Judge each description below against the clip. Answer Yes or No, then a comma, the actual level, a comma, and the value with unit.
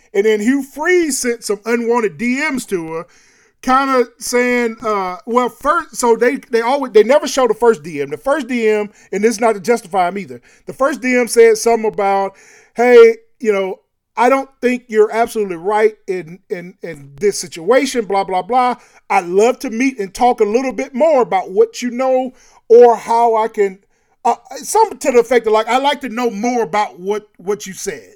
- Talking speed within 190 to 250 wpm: Yes, average, 200 wpm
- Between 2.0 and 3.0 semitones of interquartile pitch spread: No, average, 3.5 semitones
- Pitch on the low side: No, high, 235 Hz